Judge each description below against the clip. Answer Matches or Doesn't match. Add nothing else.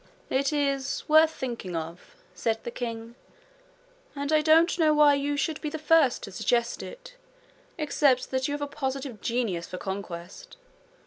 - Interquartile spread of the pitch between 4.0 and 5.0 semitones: Matches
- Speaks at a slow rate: Doesn't match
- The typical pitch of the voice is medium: Doesn't match